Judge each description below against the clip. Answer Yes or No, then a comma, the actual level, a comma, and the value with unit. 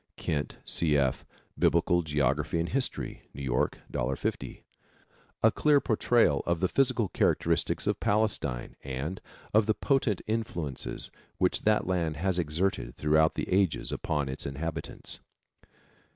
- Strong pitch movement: Yes, wide, 6.3 semitones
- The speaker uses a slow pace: Yes, slow, 130 wpm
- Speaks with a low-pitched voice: Yes, very low, 85 Hz